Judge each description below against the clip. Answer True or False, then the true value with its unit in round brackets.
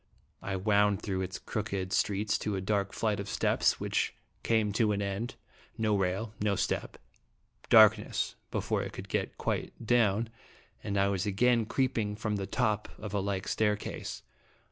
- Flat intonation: True (1.7 semitones)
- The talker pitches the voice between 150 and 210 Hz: False (105 Hz)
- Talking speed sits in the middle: True (165 wpm)